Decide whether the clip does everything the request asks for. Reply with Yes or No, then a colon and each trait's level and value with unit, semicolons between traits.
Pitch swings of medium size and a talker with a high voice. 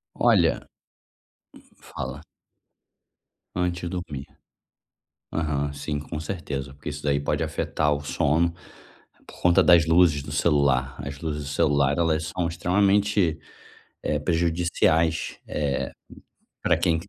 No: average, 3.1 semitones; very low, 80 Hz